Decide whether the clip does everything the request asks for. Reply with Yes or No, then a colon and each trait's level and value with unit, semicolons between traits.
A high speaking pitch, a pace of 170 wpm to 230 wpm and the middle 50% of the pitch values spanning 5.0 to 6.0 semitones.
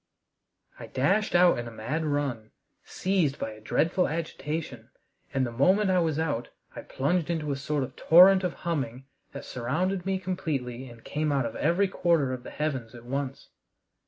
No: medium, 150 Hz; average, 180 wpm; average, 5.3 semitones